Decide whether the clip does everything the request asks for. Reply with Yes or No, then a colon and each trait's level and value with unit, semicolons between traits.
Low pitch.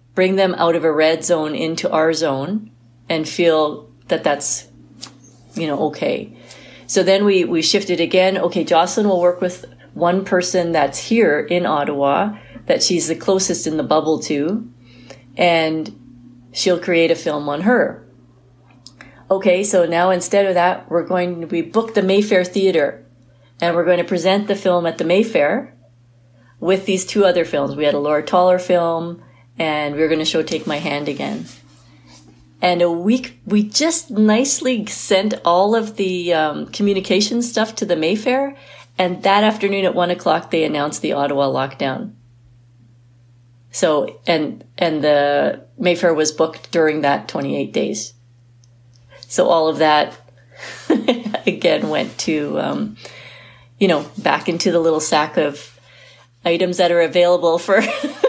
No: medium, 170 Hz